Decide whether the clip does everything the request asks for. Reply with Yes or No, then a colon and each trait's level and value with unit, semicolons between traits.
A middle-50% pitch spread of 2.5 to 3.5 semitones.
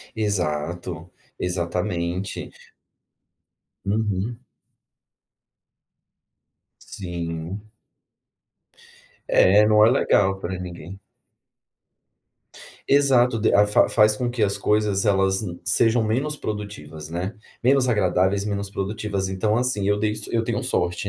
Yes: average, 3.2 semitones